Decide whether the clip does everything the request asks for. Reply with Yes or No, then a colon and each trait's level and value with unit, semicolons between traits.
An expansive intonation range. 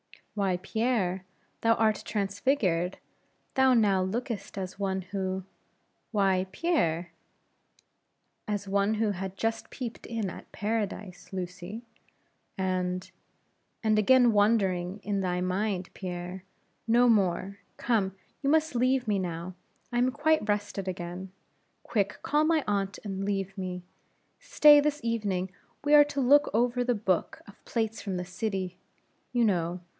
No: average, 3.8 semitones